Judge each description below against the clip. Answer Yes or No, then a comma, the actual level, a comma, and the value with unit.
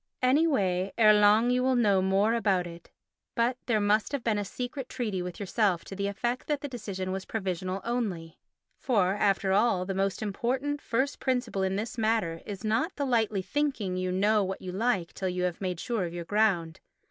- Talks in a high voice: Yes, high, 205 Hz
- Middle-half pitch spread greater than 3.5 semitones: Yes, average, 4.2 semitones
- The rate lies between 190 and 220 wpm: Yes, fast, 205 wpm